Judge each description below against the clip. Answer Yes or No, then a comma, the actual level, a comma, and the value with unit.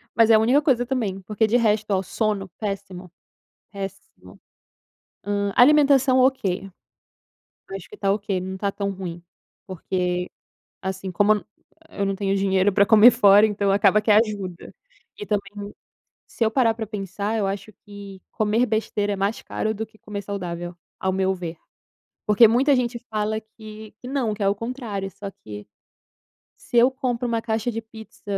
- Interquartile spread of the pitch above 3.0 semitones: No, narrow, 2.5 semitones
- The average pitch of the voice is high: Yes, high, 205 Hz